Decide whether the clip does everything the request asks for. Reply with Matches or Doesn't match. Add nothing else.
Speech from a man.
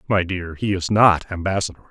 Matches